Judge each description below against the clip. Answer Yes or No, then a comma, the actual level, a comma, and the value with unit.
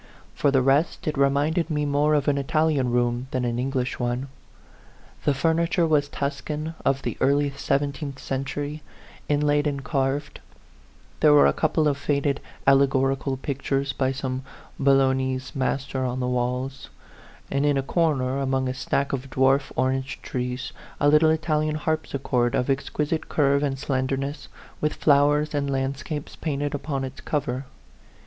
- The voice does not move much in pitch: Yes, narrow, 1.8 semitones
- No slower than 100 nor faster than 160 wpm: Yes, average, 155 wpm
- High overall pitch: No, medium, 140 Hz